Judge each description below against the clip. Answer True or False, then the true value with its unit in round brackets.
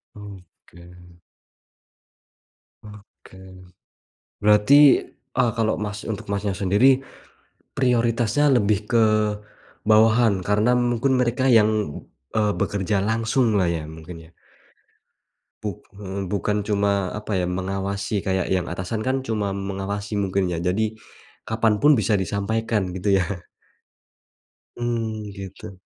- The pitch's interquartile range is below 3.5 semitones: True (2.6 semitones)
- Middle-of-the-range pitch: False (105 Hz)